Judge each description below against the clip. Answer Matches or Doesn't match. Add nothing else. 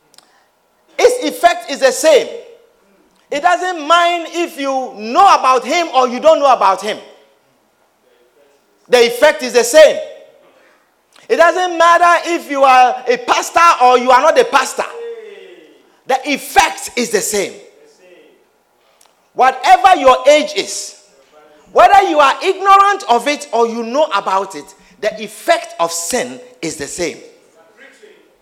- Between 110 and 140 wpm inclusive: Matches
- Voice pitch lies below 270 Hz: Doesn't match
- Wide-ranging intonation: Matches